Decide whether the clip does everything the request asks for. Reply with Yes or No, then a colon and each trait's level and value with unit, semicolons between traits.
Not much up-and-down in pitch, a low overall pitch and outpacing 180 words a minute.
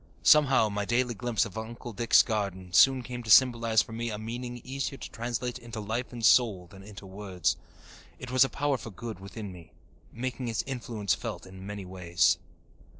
No: average, 3.7 semitones; low, 115 Hz; average, 190 wpm